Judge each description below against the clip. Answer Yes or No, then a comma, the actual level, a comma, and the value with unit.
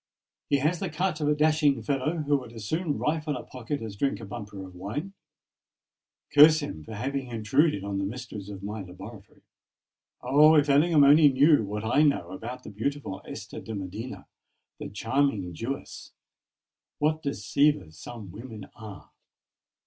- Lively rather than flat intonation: Yes, wide, 6.3 semitones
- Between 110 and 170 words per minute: Yes, average, 160 wpm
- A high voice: No, low, 130 Hz